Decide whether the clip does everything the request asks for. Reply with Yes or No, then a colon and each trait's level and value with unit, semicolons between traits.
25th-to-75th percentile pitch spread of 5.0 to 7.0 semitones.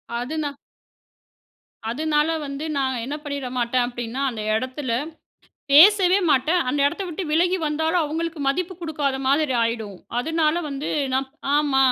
No: average, 3.6 semitones